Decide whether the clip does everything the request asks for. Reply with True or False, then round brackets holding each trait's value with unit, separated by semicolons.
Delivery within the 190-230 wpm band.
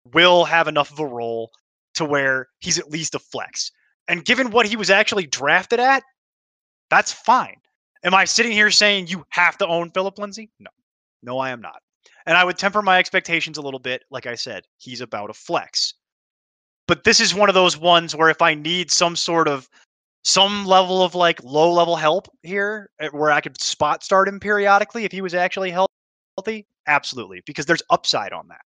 True (200 wpm)